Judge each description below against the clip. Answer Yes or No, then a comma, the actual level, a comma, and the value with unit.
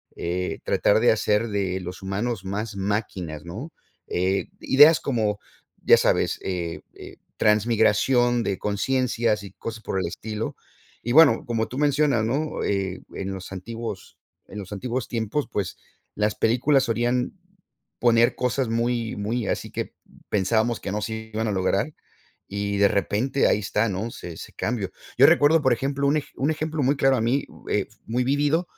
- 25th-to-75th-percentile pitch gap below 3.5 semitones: No, average, 3.9 semitones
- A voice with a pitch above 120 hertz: No, low, 110 Hz